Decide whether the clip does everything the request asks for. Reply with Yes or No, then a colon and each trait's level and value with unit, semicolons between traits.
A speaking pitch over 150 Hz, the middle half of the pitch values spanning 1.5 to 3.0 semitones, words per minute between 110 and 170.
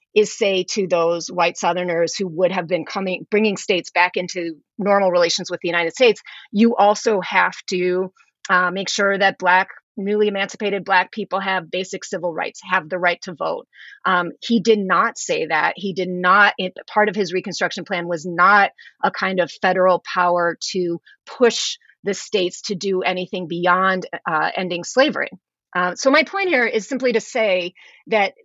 No: medium, 185 Hz; average, 2.7 semitones; average, 180 wpm